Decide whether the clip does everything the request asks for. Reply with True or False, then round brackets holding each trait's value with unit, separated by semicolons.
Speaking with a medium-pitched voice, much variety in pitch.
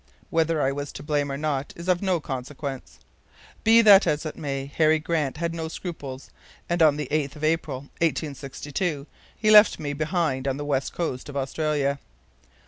False (150 Hz; 3.0 semitones)